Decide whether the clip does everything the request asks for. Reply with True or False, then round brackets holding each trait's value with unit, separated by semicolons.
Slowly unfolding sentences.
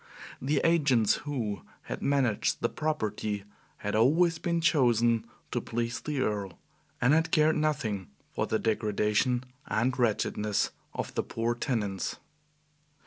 True (130 wpm)